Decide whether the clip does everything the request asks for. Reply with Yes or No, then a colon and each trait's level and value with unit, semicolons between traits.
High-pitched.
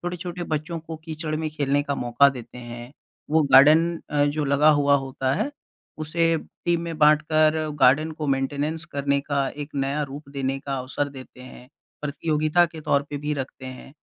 No: medium, 145 Hz